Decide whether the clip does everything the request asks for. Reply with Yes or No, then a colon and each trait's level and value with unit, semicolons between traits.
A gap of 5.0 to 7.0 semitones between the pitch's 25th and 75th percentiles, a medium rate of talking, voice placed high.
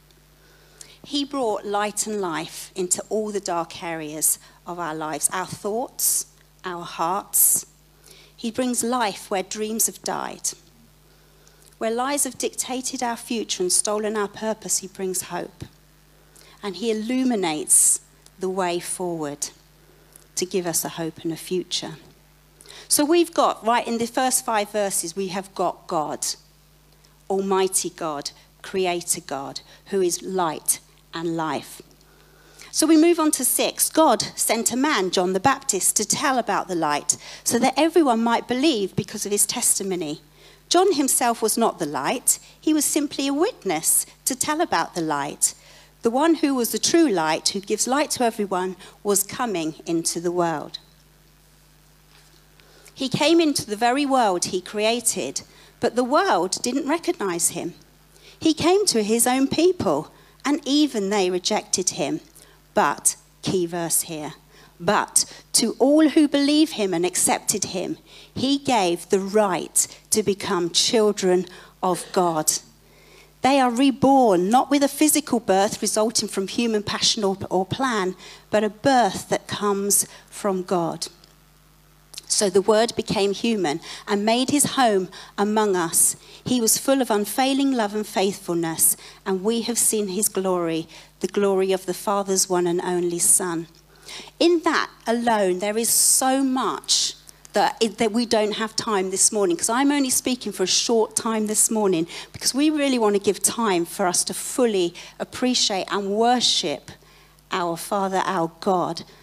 Yes: average, 5.3 semitones; average, 155 wpm; high, 205 Hz